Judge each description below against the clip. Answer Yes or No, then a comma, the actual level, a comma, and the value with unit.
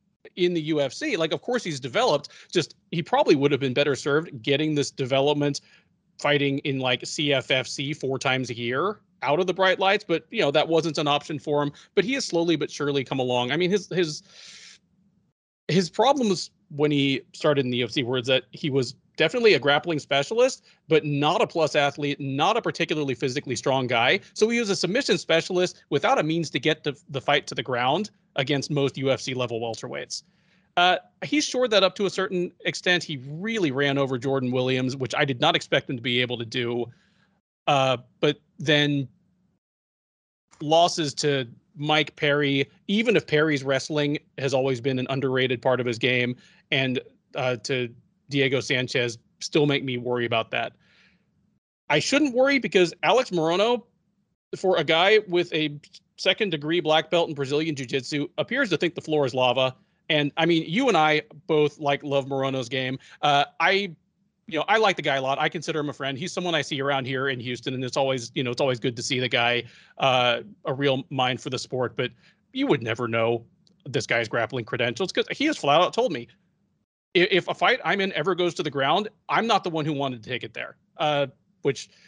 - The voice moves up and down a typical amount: Yes, average, 4.7 semitones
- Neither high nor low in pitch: Yes, medium, 145 Hz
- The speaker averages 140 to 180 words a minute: No, average, 200 wpm